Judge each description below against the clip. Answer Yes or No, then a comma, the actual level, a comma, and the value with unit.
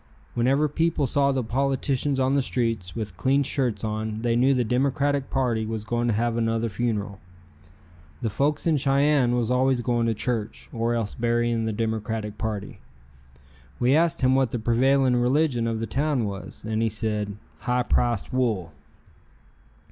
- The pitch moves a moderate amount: Yes, average, 3.2 semitones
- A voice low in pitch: Yes, low, 120 Hz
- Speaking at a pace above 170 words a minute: No, average, 165 wpm